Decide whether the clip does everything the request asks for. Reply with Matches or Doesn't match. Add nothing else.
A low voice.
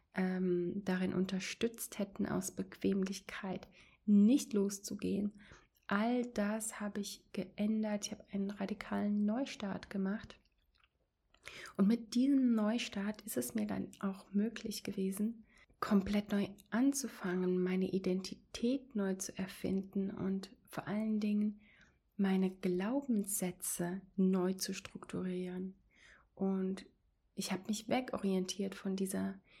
Doesn't match